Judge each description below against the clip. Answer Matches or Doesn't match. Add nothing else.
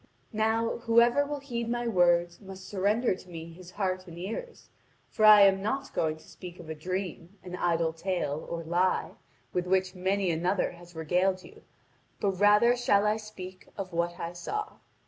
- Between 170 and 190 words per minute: Matches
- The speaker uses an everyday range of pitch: Matches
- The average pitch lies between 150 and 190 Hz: Matches